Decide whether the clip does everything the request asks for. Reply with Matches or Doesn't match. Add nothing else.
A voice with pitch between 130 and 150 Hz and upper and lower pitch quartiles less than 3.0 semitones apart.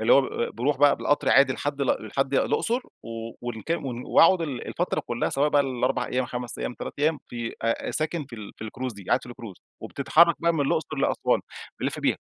Doesn't match